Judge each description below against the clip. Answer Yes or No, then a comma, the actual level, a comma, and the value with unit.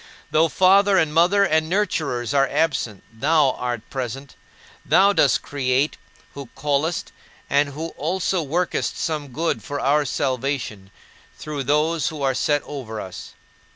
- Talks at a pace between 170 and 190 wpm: No, average, 140 wpm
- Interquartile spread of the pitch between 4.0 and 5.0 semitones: No, average, 3.4 semitones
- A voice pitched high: No, medium, 145 Hz